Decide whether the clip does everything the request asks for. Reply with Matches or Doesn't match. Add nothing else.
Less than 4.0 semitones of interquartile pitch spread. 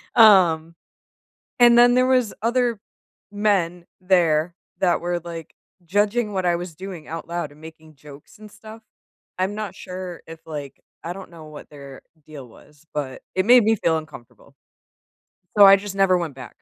Doesn't match